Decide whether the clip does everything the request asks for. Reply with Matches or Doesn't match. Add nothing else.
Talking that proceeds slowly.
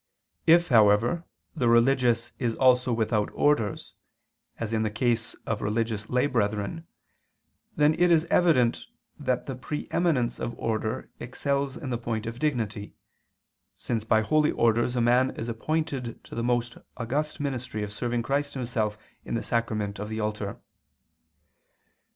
Doesn't match